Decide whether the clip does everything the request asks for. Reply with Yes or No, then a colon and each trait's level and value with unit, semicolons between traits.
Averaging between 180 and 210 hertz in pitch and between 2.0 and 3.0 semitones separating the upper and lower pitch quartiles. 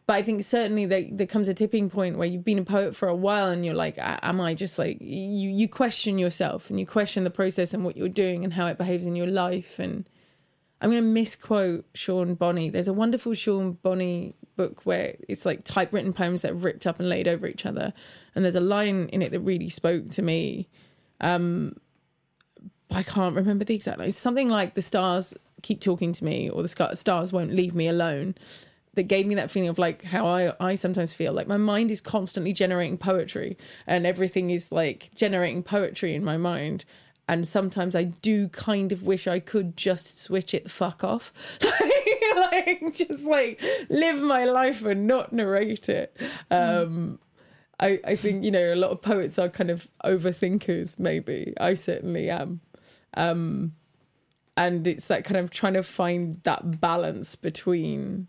Yes: medium, 185 Hz; average, 2.7 semitones